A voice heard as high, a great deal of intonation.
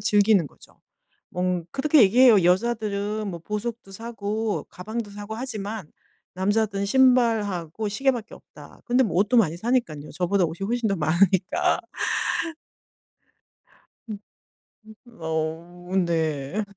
No: high, 205 Hz; average, 4.1 semitones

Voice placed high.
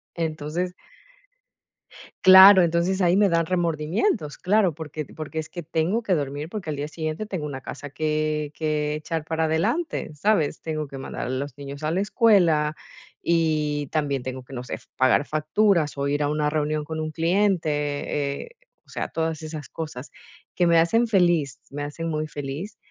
No: medium, 155 Hz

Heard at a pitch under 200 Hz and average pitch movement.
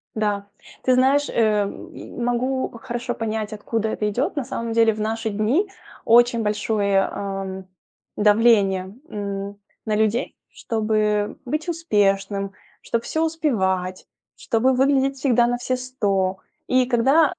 No: high, 225 Hz; average, 3.9 semitones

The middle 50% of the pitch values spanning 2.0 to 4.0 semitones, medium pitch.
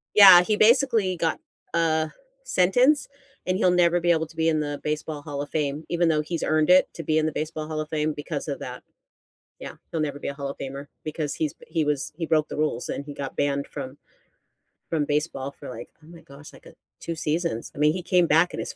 Yes: average, 2.8 semitones; medium, 155 Hz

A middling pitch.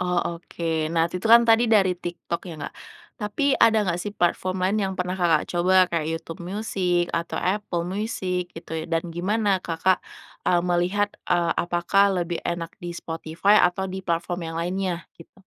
Yes: medium, 180 Hz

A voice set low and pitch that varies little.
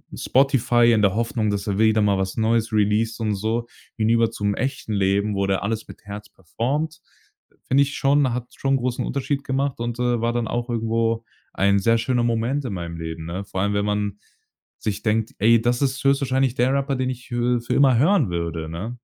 No: low, 115 Hz; average, 3.7 semitones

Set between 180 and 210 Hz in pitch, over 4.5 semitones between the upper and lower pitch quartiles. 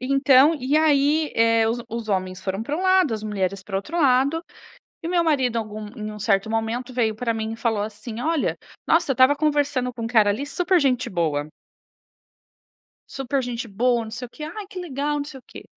No: very high, 250 Hz; average, 4.9 semitones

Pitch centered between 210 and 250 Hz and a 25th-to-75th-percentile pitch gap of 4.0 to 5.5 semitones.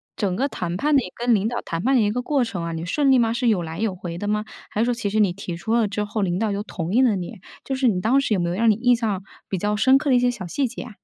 Yes: high, 215 Hz; average, 4.7 semitones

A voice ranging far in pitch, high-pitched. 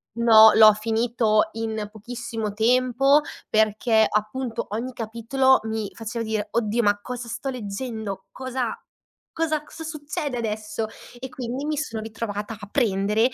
No: average, 2.8 semitones; high, 225 Hz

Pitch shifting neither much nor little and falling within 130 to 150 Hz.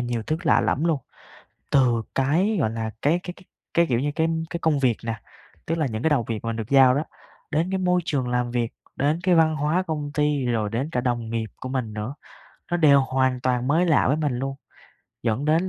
Yes: average, 4.7 semitones; low, 135 Hz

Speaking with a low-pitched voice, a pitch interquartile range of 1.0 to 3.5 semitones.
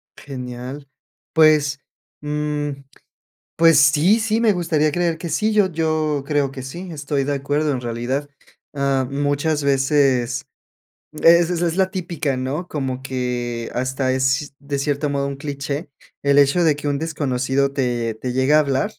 No: medium, 145 Hz; average, 2.8 semitones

